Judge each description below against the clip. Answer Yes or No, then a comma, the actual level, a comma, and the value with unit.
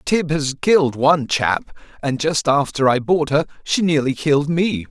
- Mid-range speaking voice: Yes, medium, 150 Hz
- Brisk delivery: No, average, 185 wpm